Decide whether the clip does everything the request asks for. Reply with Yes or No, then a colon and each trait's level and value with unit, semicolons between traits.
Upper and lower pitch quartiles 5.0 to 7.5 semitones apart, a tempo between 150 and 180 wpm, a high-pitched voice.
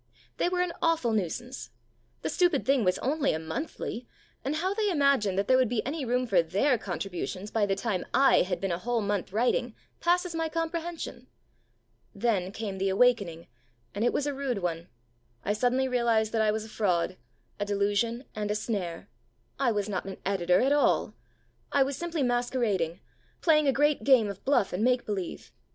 No: wide, 5.6 semitones; average, 190 wpm; high, 230 Hz